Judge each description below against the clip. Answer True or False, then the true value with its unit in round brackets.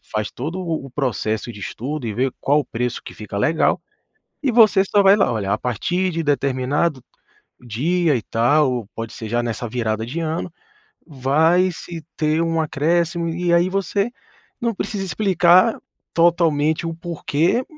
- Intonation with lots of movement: True (5.9 semitones)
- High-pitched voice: False (155 Hz)